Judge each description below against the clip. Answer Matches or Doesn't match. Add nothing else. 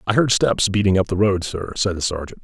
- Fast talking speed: Matches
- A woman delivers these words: Doesn't match